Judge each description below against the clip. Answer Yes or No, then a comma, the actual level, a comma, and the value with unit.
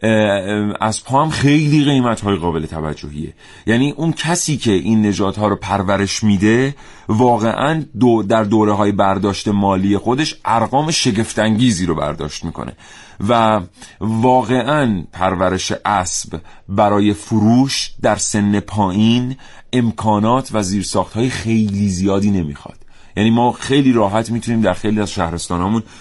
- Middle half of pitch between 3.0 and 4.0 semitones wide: Yes, average, 3.4 semitones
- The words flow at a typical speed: Yes, average, 125 wpm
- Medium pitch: No, low, 110 Hz